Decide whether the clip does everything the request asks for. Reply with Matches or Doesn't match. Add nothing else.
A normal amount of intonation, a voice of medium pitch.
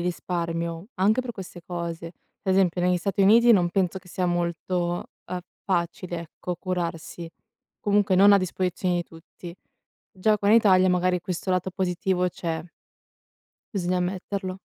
Doesn't match